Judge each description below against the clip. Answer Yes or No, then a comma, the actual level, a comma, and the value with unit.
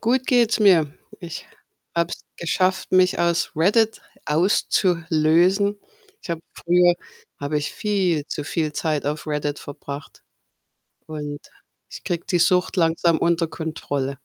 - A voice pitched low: No, medium, 170 Hz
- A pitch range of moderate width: Yes, average, 3.2 semitones